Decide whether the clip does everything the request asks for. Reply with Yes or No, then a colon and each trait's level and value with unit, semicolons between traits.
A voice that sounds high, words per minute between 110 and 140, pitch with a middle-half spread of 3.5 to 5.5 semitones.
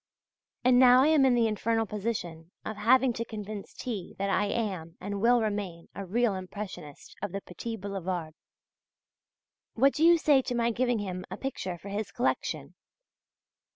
No: high, 215 Hz; average, 170 wpm; average, 4.2 semitones